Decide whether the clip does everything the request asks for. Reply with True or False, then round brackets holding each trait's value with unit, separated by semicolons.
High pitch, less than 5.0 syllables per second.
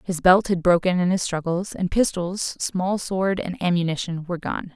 False (180 Hz; 4.8 syllables/s)